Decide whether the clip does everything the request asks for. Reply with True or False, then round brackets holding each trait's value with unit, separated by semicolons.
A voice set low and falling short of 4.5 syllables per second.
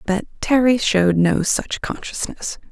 False (210 Hz; 4.0 syllables/s)